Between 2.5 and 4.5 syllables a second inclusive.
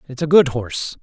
No: 5.9 syllables/s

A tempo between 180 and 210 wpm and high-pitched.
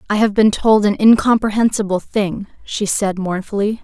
No: average, 155 wpm; high, 205 Hz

